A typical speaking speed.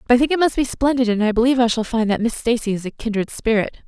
No: fast, 310 wpm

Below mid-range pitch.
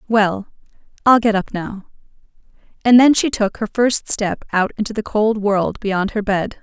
No: high, 210 Hz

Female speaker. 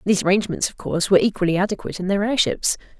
Yes: female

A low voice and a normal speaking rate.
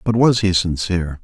Yes: very low, 95 Hz; average, 195 wpm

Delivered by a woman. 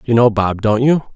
No: male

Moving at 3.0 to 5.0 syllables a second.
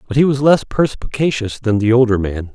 No: 5.4 syllables/s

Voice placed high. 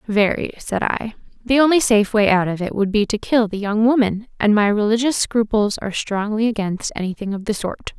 Yes: high, 215 Hz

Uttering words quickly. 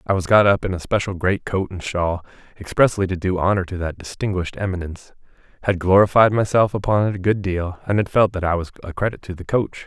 Yes: fast, 230 wpm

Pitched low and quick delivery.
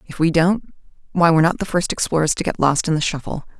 No: medium, 165 Hz; fast, 250 wpm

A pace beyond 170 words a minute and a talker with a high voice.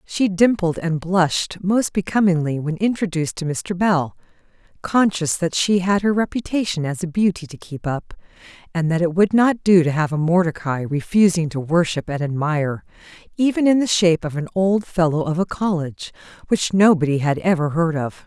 No: average, 180 wpm; medium, 175 Hz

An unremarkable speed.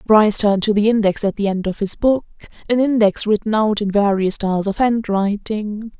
Yes: average, 190 wpm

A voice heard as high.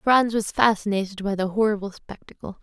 Yes: high, 205 Hz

